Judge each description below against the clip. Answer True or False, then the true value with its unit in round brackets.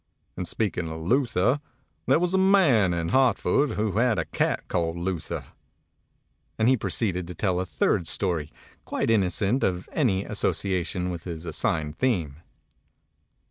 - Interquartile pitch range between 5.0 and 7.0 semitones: True (5.6 semitones)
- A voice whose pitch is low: True (95 Hz)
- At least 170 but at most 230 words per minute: False (150 wpm)